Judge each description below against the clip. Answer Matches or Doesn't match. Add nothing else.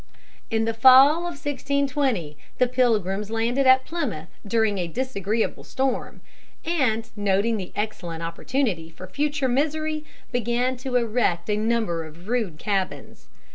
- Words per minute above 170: Doesn't match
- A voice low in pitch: Doesn't match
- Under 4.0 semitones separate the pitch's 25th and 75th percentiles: Doesn't match